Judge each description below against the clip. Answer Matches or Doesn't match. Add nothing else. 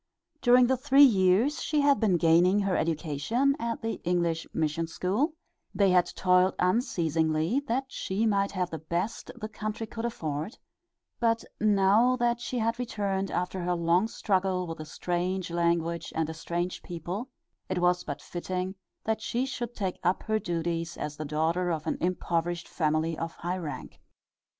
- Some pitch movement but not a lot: Matches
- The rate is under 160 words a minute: Doesn't match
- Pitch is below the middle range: Doesn't match